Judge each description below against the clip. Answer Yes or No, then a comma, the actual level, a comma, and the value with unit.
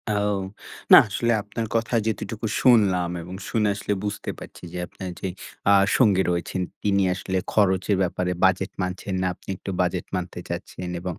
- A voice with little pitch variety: Yes, narrow, 2.2 semitones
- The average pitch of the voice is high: No, very low, 95 Hz